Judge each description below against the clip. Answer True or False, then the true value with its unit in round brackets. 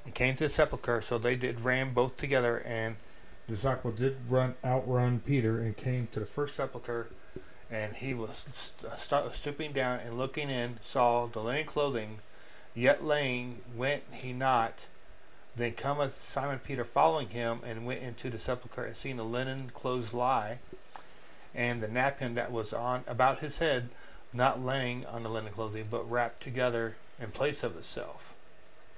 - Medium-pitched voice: False (125 Hz)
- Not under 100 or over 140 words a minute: False (170 wpm)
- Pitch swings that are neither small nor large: False (2.1 semitones)